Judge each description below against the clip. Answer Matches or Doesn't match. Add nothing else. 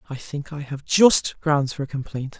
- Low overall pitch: Doesn't match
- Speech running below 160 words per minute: Doesn't match